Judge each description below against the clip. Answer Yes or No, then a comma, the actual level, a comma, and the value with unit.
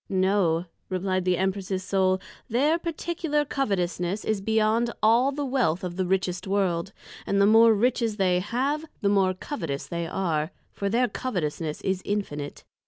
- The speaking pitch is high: Yes, high, 195 Hz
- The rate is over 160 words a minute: No, average, 155 wpm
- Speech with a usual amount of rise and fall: Yes, average, 4.1 semitones